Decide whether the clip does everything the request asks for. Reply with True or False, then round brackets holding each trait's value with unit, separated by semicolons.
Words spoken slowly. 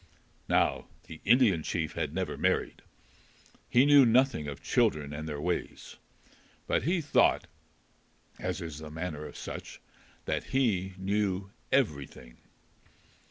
True (125 wpm)